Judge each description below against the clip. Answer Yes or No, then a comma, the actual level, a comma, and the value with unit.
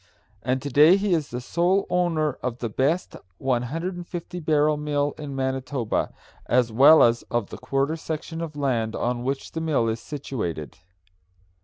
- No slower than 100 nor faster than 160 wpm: Yes, average, 155 wpm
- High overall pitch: No, medium, 145 Hz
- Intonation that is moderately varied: Yes, average, 4.5 semitones